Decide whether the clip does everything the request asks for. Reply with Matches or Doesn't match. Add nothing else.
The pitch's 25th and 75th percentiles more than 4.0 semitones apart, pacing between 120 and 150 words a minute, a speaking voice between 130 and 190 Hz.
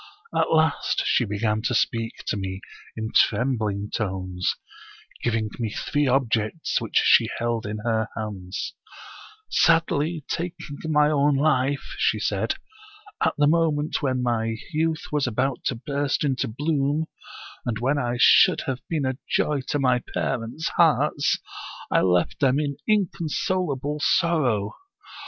Matches